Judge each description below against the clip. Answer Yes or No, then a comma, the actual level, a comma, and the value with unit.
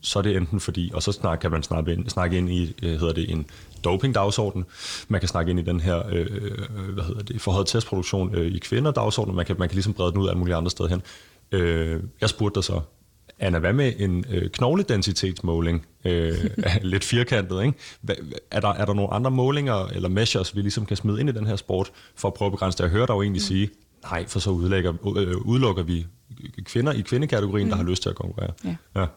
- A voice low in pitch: Yes, low, 100 Hz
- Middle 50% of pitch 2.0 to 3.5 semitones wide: Yes, average, 3.0 semitones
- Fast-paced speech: No, average, 210 wpm